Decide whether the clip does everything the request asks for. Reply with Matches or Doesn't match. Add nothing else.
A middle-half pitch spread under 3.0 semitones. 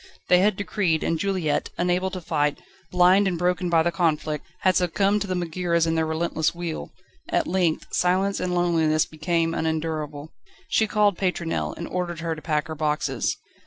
Matches